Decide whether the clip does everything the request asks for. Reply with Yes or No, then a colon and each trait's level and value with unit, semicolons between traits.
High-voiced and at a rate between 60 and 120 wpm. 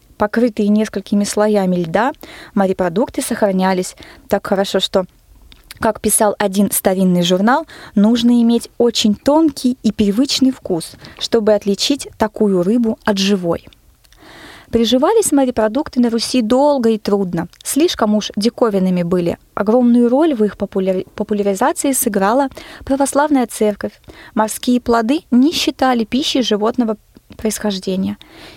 Yes: high, 220 Hz; average, 115 wpm